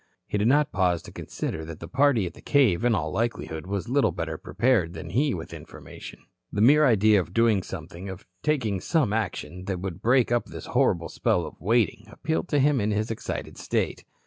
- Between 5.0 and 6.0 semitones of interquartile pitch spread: Yes, wide, 5.6 semitones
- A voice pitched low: Yes, low, 105 Hz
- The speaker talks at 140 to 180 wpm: No, fast, 205 wpm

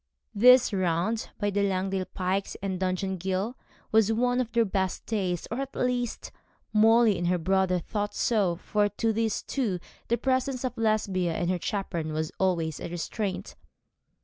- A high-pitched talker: Yes, high, 200 Hz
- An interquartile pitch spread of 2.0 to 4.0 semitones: Yes, average, 3.6 semitones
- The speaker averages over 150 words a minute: Yes, average, 165 wpm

